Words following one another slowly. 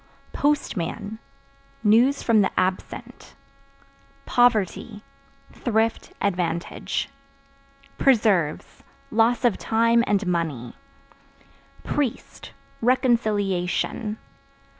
Yes: slow, 65 wpm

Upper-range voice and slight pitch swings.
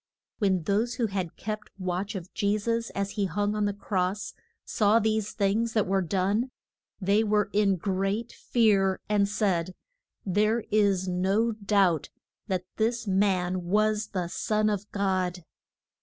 Yes: high, 200 Hz; narrow, 2.2 semitones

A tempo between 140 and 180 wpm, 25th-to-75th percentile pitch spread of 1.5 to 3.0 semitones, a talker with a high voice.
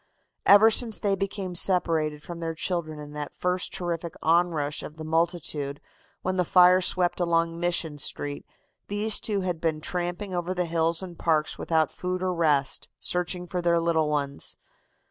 No: average, 165 wpm; narrow, 2.5 semitones; medium, 170 Hz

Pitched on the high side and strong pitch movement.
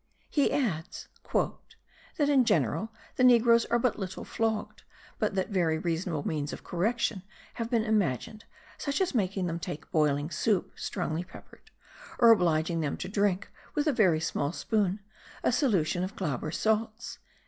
Yes: high, 195 Hz; wide, 5.7 semitones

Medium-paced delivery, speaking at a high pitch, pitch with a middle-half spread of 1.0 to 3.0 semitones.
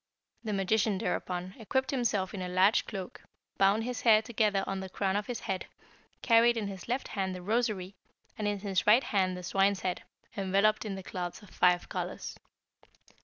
Yes: average, 180 wpm; high, 200 Hz; narrow, 2.6 semitones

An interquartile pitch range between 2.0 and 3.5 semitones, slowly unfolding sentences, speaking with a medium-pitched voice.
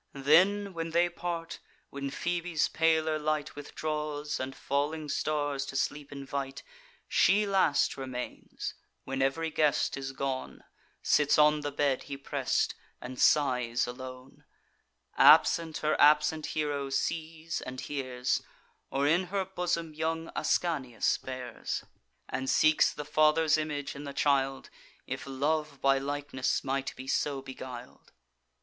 Yes: average, 2.7 semitones; slow, 130 wpm; medium, 145 Hz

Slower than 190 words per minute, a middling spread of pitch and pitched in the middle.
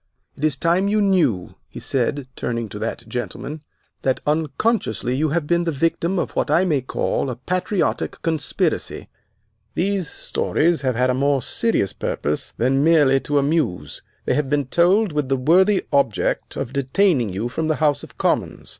Yes: average, 170 wpm; average, 5.0 semitones; medium, 145 Hz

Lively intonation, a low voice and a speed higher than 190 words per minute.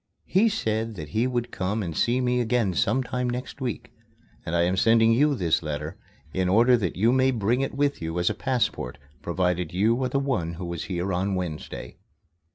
Yes: wide, 6.0 semitones; low, 110 Hz; average, 200 wpm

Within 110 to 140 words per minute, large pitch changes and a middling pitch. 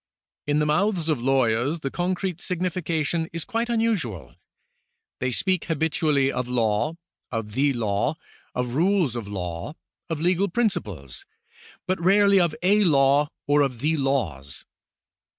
Yes: slow, 135 wpm; wide, 6.3 semitones; medium, 150 Hz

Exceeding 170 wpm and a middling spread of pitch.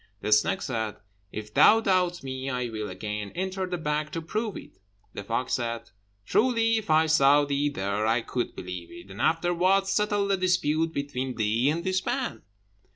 No: average, 180 wpm; wide, 8.1 semitones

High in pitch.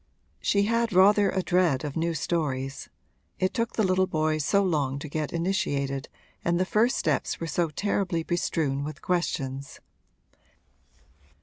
No: medium, 170 Hz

